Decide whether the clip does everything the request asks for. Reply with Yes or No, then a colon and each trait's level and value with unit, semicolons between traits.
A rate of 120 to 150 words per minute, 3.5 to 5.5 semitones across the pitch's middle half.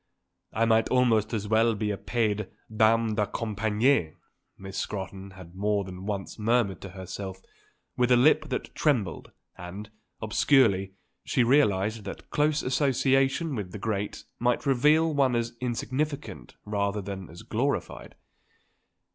Yes: average, 140 wpm; average, 4.2 semitones